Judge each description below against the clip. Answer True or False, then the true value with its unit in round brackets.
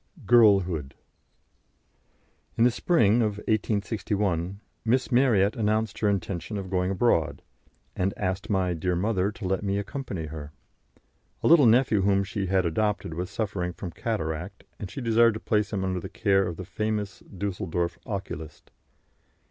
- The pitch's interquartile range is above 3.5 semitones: False (3.1 semitones)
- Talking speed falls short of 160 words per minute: True (150 wpm)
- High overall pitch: False (100 Hz)